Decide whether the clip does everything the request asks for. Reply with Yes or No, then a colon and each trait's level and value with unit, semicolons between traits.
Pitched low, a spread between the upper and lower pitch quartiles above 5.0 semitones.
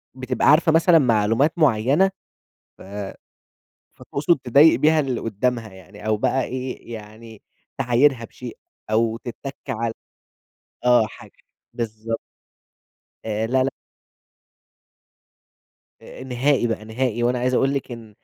No: low, 120 Hz; average, 3.2 semitones